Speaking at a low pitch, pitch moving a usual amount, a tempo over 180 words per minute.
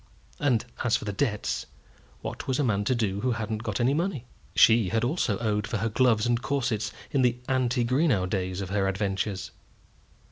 Yes: low, 115 Hz; average, 3.7 semitones; average, 190 wpm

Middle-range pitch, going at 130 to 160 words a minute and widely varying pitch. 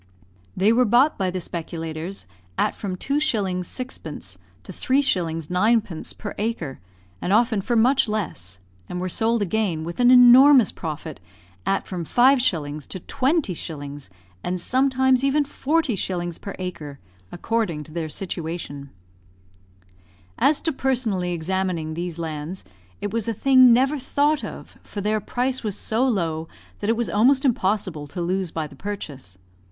No: high, 195 Hz; average, 145 wpm; wide, 6.9 semitones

